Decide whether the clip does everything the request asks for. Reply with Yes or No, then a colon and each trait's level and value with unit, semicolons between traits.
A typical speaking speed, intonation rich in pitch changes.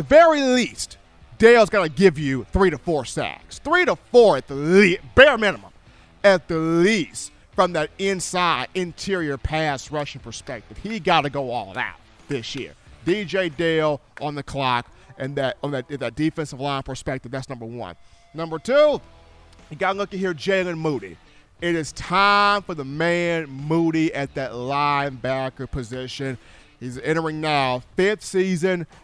Yes: average, 155 wpm; wide, 5.7 semitones